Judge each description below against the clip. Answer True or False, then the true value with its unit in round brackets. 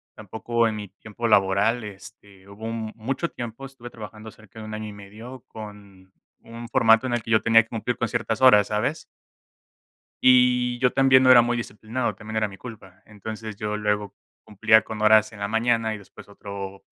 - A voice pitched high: False (110 Hz)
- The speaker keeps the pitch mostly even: True (2.3 semitones)